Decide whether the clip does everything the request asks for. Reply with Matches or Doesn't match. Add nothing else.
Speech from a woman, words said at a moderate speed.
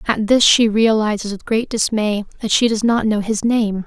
Doesn't match